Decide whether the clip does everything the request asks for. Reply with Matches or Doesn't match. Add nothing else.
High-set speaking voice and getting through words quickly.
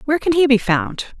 Matches